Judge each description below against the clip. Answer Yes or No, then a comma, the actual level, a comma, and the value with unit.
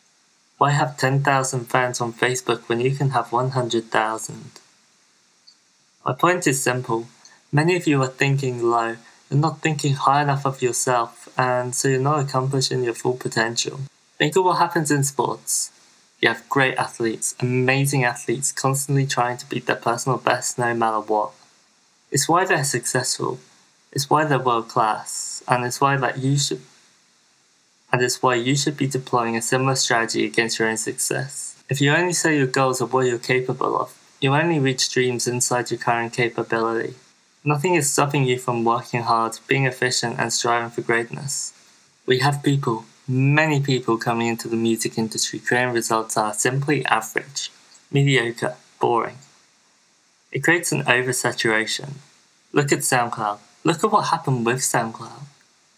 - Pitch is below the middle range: Yes, low, 125 Hz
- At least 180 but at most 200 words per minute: No, average, 165 wpm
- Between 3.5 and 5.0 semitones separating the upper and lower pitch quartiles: No, average, 2.9 semitones